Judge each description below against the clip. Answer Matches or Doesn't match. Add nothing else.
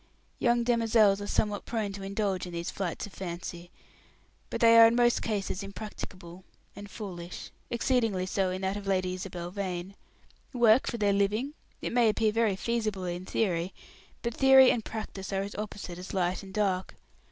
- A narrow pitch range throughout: Doesn't match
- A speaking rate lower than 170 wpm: Doesn't match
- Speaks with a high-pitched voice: Matches